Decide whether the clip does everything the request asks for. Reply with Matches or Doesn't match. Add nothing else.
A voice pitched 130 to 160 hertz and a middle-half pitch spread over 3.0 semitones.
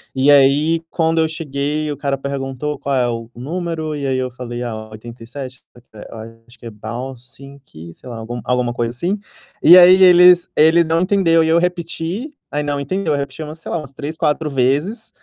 Matches